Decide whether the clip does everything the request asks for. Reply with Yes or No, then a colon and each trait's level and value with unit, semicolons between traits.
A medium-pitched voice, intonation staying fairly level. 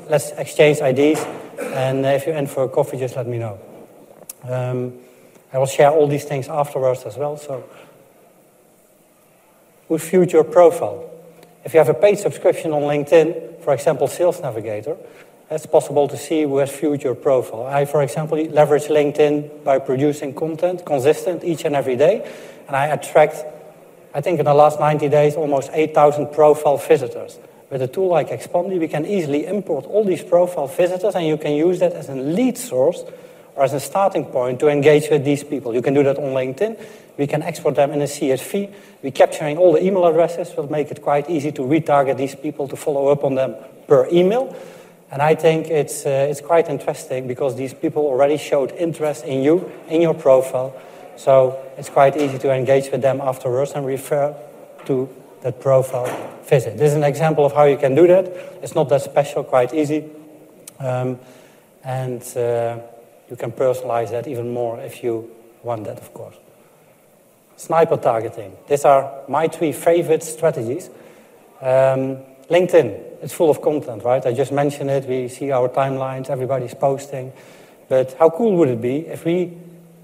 No: medium, 145 Hz; average, 3.3 semitones